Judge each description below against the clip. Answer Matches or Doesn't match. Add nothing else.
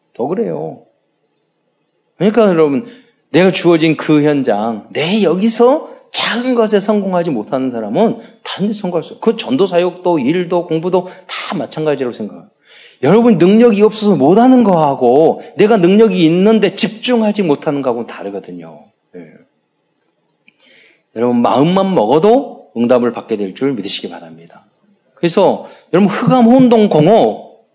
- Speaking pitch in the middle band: Matches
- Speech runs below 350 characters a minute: Matches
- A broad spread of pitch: Matches